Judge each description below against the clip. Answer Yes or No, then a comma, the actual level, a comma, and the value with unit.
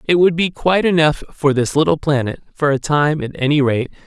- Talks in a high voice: No, medium, 150 Hz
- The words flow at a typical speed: No, fast, 220 wpm